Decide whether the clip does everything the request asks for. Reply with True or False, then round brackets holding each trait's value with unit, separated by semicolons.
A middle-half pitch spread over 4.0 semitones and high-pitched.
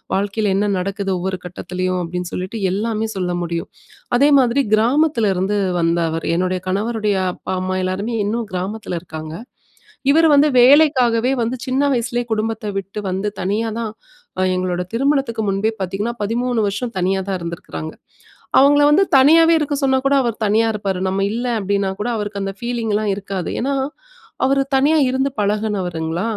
True (4.5 semitones; 210 Hz)